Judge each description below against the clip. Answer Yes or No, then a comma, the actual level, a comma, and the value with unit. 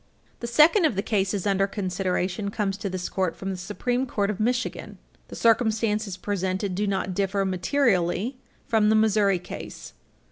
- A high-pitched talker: Yes, high, 200 Hz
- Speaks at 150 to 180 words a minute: Yes, average, 165 wpm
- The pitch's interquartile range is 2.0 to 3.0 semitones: Yes, narrow, 2.6 semitones